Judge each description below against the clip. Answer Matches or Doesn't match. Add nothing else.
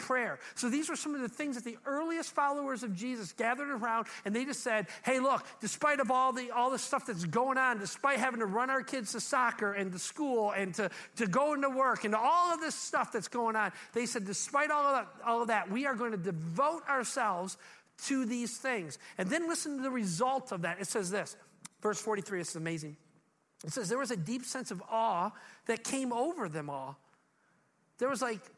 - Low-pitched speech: Doesn't match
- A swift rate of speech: Matches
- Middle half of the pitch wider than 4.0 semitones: Matches